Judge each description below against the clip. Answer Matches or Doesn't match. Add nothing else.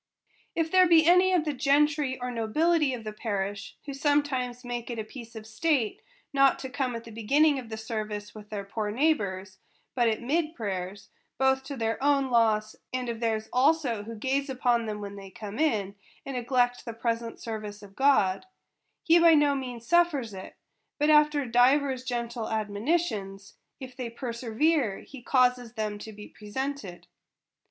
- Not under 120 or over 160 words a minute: Doesn't match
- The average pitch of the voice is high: Matches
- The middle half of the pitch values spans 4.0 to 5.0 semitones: Matches